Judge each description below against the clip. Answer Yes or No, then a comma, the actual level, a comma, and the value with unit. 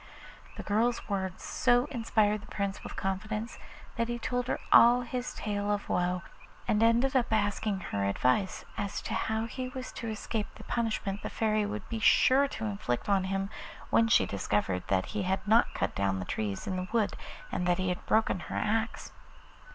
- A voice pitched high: Yes, high, 210 Hz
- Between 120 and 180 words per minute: No, average, 195 wpm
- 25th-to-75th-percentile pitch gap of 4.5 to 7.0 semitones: No, average, 3.4 semitones